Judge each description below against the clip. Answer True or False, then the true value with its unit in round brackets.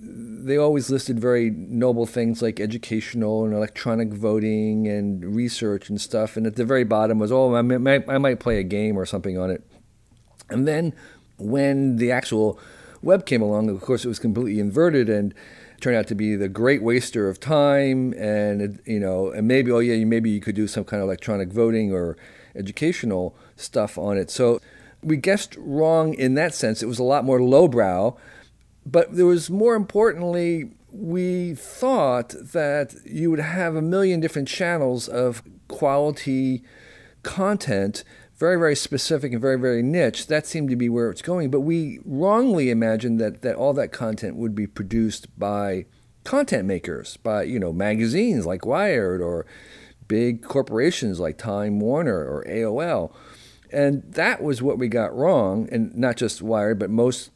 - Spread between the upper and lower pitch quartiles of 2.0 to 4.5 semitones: False (4.9 semitones)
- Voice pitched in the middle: False (120 Hz)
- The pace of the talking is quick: False (170 wpm)